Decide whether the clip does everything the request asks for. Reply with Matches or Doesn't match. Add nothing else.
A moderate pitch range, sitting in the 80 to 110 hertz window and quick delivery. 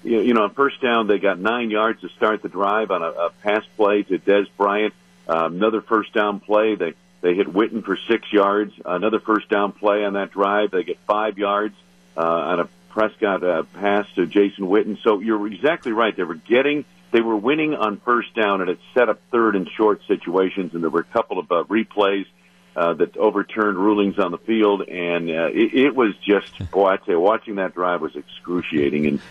Matches